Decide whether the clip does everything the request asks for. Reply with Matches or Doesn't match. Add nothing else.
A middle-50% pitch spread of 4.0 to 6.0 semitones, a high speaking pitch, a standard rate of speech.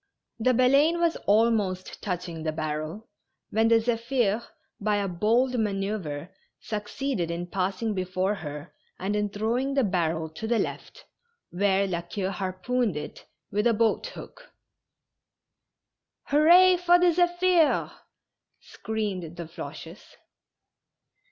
Doesn't match